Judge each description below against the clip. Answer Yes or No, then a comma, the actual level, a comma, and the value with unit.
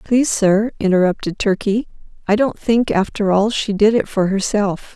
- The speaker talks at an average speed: Yes, average, 170 wpm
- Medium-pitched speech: No, high, 205 Hz